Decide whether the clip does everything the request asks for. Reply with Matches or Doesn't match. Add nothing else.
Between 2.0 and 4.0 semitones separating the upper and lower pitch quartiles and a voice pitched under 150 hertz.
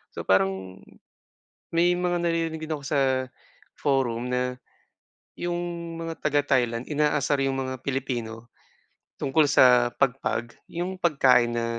Doesn't match